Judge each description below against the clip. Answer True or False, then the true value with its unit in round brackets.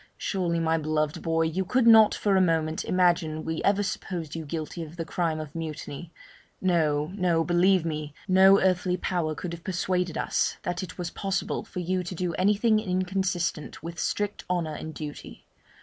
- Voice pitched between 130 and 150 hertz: False (175 Hz)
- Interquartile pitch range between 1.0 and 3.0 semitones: True (2.6 semitones)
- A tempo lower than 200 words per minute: True (180 wpm)